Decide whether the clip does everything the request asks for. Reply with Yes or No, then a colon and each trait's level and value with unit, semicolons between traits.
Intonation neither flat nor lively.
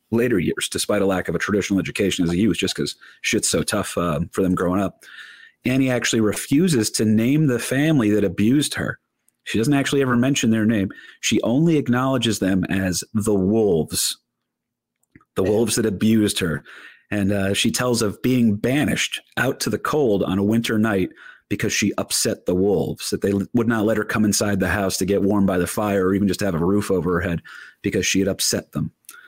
Yes: average, 3.1 semitones